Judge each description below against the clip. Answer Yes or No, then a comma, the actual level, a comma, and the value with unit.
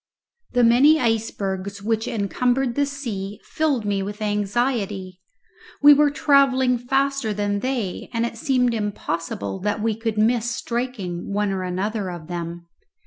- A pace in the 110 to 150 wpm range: Yes, average, 140 wpm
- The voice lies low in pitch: No, high, 220 Hz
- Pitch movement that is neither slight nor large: Yes, average, 4.1 semitones